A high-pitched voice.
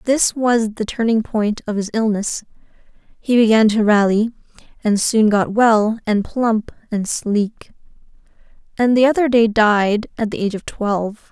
Yes: high, 220 Hz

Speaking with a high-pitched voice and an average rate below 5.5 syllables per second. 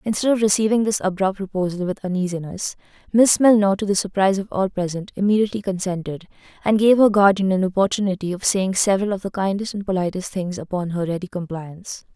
No: high, 195 Hz; 6.2 syllables/s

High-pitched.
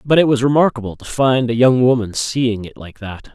No: low, 120 Hz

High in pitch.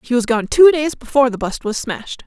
Yes: very high, 250 Hz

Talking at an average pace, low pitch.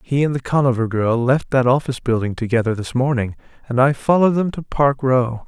No: fast, 210 wpm; low, 130 Hz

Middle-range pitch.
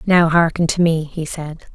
Yes: medium, 165 Hz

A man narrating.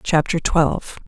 No: female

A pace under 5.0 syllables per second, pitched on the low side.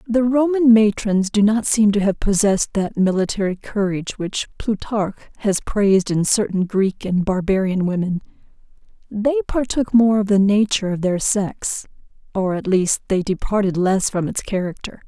No: 4.8 syllables/s; high, 205 Hz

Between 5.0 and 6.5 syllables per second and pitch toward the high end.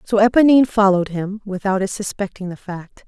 Yes: 5.8 syllables/s; high, 200 Hz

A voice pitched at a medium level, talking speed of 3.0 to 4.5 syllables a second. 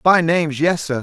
No: medium, 160 Hz; 5.4 syllables/s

